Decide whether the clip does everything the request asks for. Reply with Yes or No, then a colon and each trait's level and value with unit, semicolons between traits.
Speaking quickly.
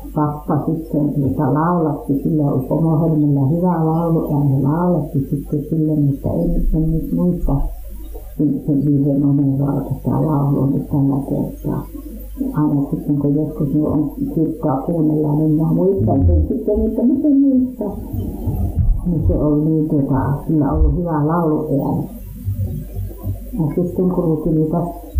No: average, 105 wpm